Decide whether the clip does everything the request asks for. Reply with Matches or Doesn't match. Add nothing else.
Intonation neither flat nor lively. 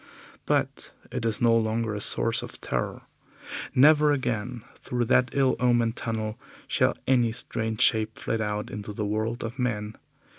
Doesn't match